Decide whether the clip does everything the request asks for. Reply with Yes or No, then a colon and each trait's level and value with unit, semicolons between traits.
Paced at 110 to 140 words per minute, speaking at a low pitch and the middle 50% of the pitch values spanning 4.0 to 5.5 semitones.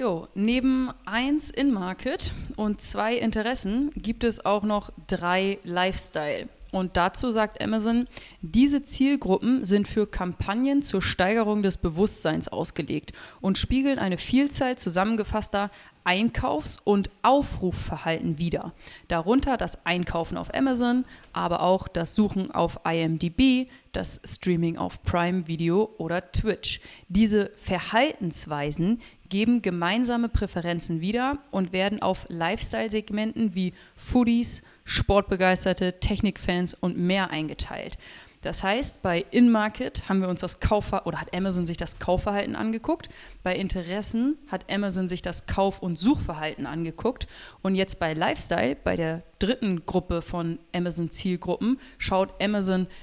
No: slow, 125 wpm; high, 195 Hz; average, 4.3 semitones